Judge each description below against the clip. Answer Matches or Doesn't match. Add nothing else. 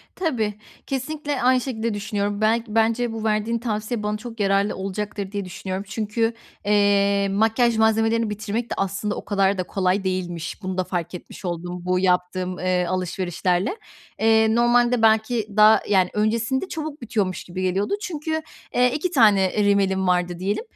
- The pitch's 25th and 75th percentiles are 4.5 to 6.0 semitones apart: Doesn't match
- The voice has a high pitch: Matches